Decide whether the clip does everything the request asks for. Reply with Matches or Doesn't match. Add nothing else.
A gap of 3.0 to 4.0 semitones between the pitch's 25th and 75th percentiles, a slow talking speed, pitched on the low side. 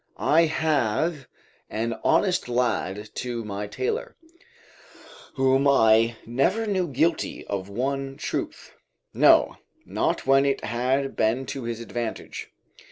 Doesn't match